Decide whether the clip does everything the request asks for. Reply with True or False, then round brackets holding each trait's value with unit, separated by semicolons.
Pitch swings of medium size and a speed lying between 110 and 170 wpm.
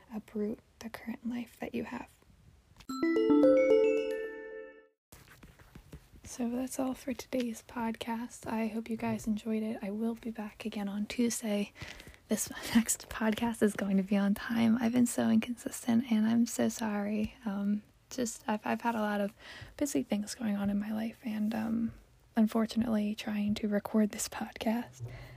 False (2.1 semitones; 155 wpm)